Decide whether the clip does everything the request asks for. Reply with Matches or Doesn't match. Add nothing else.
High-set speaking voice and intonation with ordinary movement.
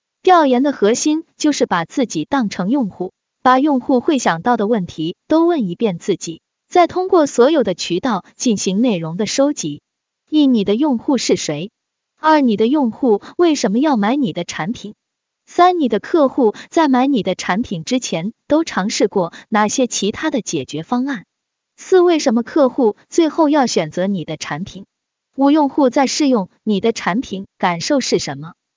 Doesn't match